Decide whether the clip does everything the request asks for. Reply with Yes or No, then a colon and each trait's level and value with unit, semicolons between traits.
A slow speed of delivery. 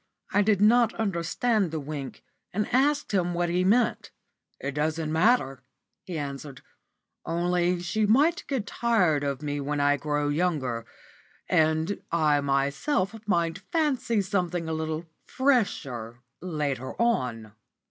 Yes: slow, 130 wpm